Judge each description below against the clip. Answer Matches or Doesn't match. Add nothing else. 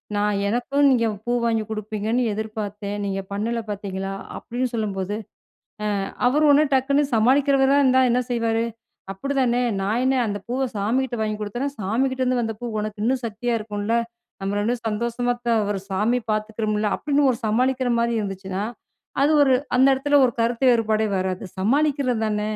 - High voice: Matches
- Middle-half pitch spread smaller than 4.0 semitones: Matches